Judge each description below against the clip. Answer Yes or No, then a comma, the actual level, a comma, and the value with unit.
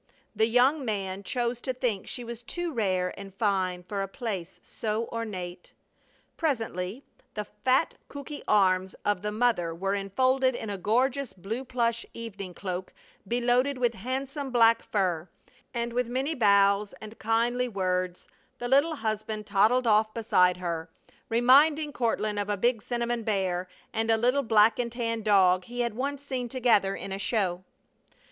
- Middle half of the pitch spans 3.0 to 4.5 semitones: Yes, average, 4.0 semitones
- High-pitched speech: Yes, high, 225 Hz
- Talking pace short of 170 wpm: Yes, average, 160 wpm